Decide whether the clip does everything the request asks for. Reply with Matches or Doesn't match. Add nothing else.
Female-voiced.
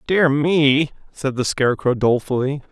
Doesn't match